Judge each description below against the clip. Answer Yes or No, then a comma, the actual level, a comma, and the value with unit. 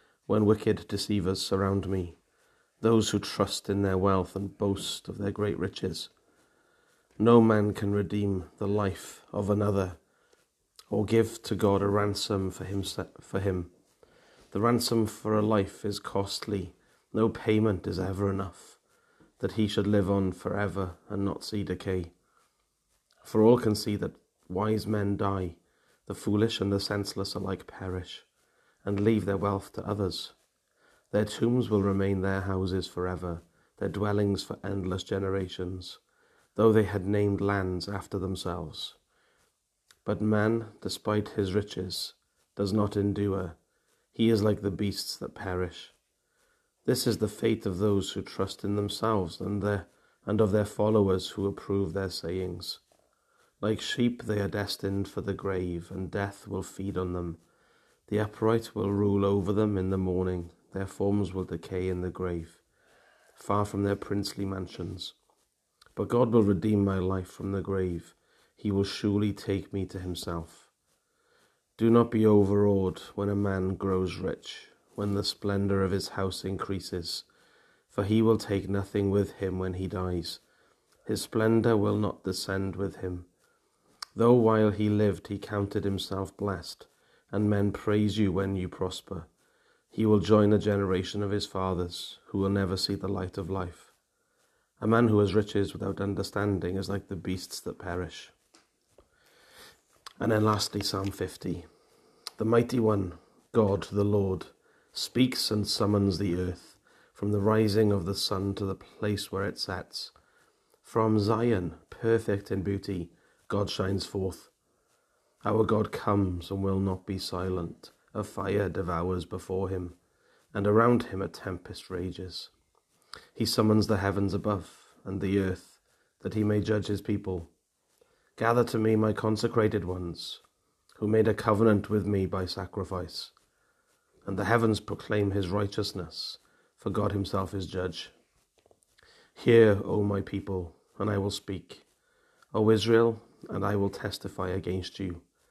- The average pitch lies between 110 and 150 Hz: No, low, 100 Hz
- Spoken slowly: No, average, 155 wpm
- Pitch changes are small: Yes, narrow, 1.9 semitones